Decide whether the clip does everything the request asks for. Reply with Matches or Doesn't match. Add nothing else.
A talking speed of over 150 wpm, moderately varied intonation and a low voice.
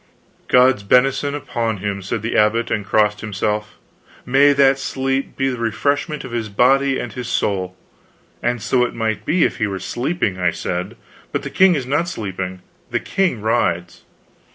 Matches